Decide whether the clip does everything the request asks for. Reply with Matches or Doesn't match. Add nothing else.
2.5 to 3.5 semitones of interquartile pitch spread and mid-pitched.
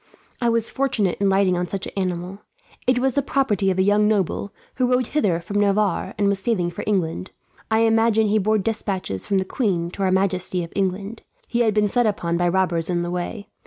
Doesn't match